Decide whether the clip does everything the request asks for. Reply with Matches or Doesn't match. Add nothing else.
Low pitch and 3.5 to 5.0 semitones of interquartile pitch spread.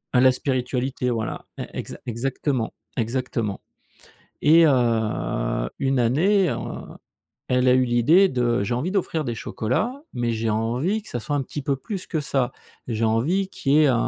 Matches